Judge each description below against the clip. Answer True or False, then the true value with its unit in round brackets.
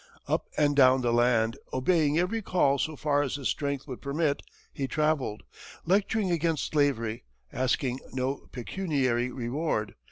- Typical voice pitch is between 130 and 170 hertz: True (140 Hz)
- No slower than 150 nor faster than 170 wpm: False (140 wpm)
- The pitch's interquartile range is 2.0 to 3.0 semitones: False (3.8 semitones)